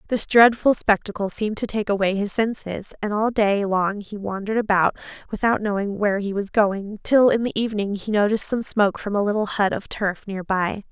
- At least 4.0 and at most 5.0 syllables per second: No, 5.5 syllables/s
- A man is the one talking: No, female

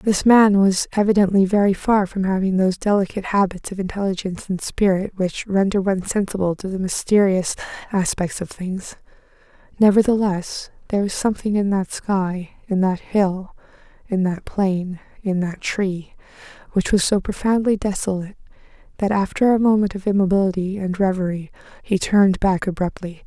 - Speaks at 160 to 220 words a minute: No, average, 150 wpm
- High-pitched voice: Yes, high, 195 Hz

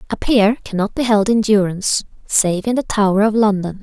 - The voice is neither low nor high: No, high, 210 Hz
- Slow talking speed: No, fast, 205 wpm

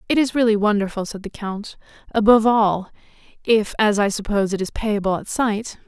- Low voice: No, high, 210 Hz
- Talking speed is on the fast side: No, average, 185 wpm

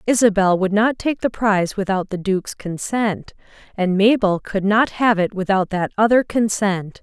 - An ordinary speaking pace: Yes, average, 160 wpm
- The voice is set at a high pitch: Yes, high, 205 Hz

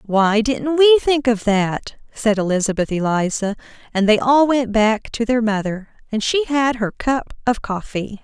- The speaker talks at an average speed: Yes, average, 175 wpm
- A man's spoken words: No, female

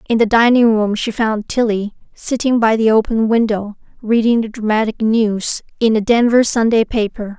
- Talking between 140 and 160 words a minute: No, average, 170 wpm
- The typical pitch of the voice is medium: No, high, 220 Hz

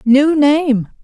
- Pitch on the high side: Yes, very high, 280 Hz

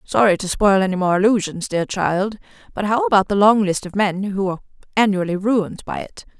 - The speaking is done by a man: No, female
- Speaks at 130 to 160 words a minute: No, fast, 205 wpm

